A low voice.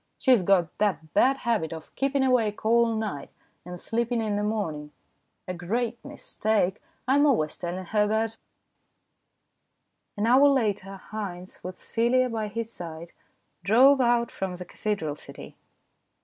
No: high, 215 Hz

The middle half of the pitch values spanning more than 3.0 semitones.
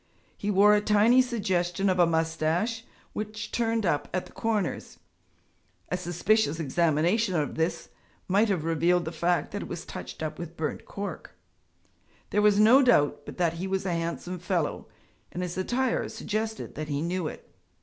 Yes: average, 4.1 semitones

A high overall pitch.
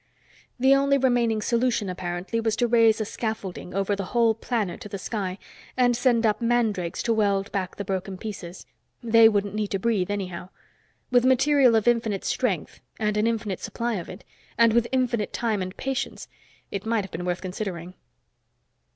Yes: high, 220 Hz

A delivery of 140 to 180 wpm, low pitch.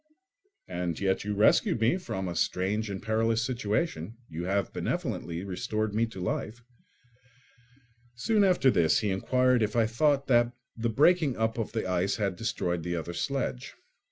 Yes: average, 160 wpm; low, 110 Hz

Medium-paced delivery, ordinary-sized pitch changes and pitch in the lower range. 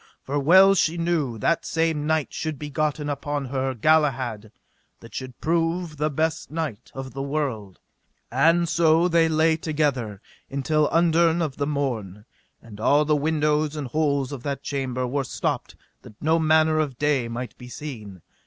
No: average, 165 wpm; average, 3.2 semitones; medium, 150 Hz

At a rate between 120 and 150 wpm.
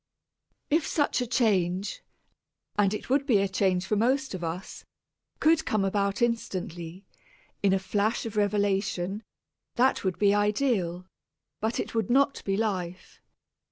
Yes: average, 145 wpm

